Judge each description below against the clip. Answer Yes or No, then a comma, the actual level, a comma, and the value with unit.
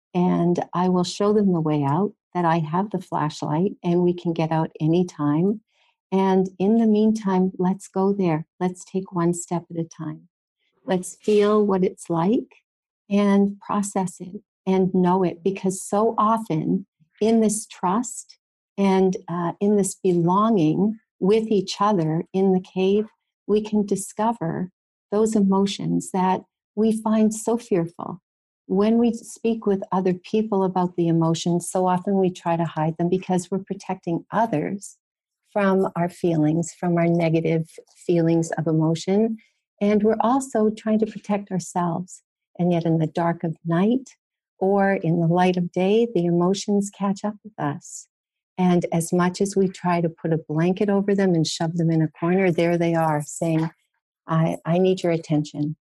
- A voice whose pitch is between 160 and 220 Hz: Yes, medium, 185 Hz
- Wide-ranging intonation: No, average, 3.3 semitones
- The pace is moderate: Yes, average, 165 wpm